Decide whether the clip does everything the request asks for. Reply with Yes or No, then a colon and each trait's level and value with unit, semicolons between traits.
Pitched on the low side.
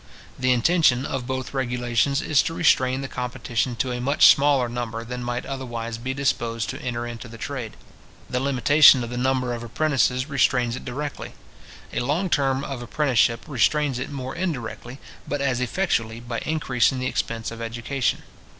Yes: low, 125 Hz